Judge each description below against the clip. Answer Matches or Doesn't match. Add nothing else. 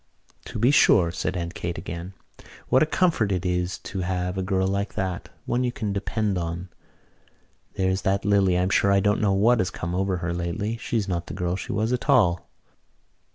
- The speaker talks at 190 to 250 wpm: Matches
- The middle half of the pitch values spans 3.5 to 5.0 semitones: Doesn't match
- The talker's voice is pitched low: Matches